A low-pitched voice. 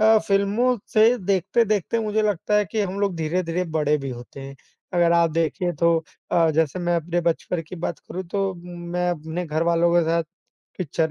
No: medium, 175 Hz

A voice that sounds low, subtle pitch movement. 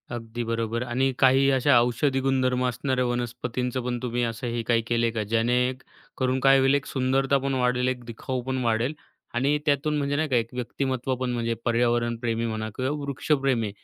Yes: low, 125 Hz; narrow, 2.1 semitones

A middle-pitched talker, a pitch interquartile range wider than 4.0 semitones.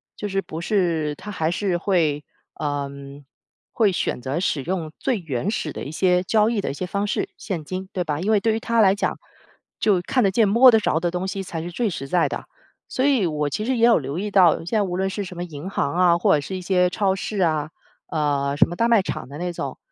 Yes: medium, 180 Hz; average, 4.4 semitones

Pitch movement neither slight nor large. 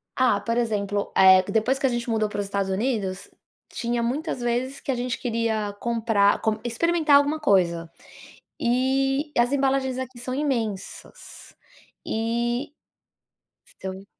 Yes: average, 4.0 semitones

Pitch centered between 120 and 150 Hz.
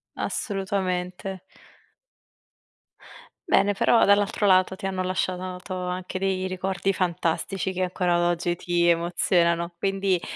No: medium, 185 Hz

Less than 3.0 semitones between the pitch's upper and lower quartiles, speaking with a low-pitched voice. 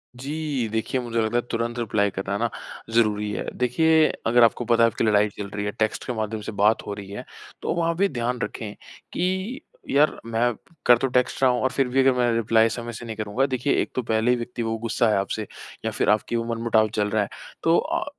Yes: narrow, 2.4 semitones; low, 115 Hz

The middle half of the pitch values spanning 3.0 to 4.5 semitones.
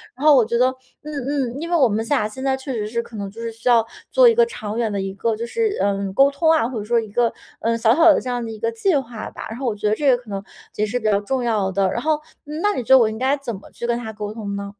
Yes: average, 4.0 semitones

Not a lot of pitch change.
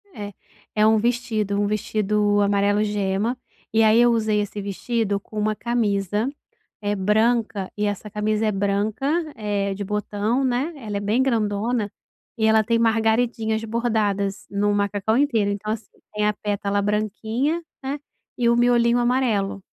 Yes: narrow, 2.2 semitones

